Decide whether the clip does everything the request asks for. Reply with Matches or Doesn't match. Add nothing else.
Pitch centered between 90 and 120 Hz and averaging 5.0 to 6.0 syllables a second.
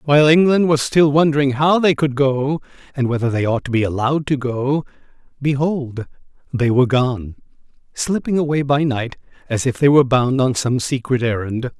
Doesn't match